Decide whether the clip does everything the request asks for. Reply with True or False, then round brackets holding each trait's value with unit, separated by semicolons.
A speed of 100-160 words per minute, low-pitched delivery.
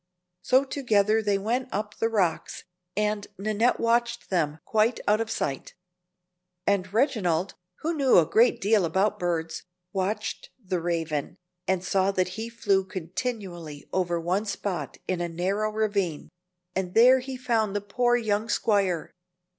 False (145 wpm; 205 Hz)